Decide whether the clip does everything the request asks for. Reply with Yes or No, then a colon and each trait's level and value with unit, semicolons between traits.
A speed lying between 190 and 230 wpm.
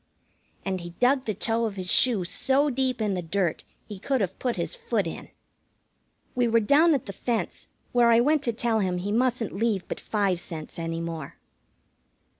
Yes: average, 195 wpm